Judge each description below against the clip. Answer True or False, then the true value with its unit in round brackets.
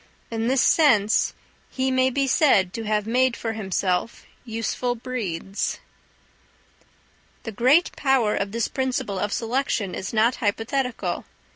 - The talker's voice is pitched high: True (230 Hz)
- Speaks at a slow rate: True (130 wpm)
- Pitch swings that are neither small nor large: True (3.8 semitones)